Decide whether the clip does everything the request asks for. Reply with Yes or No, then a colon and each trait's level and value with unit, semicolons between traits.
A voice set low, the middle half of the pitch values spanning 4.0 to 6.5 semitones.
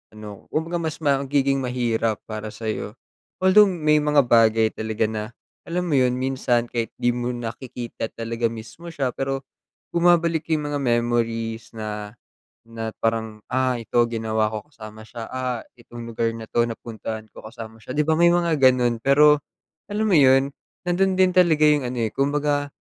Yes: low, 125 Hz; average, 4.6 semitones